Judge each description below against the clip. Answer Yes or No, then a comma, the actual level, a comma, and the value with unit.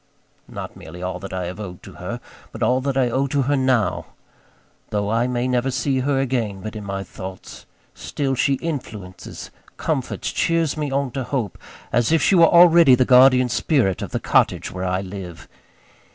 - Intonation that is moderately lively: No, wide, 5.8 semitones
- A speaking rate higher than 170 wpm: Yes, average, 190 wpm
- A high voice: No, low, 125 Hz